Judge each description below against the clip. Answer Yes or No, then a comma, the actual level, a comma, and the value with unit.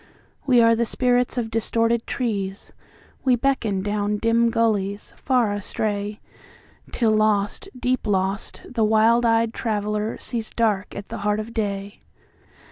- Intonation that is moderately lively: No, narrow, 2.1 semitones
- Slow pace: Yes, slow, 125 wpm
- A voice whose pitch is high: Yes, high, 220 Hz